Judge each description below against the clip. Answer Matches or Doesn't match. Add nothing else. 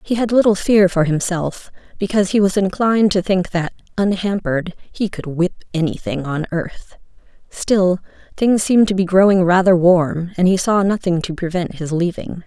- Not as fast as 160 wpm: Doesn't match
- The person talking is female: Matches